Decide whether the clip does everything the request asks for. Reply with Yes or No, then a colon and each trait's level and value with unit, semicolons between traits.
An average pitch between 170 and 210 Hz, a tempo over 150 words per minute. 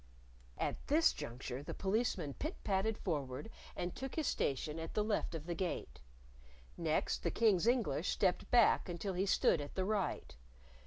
Yes: high, 190 Hz; average, 165 wpm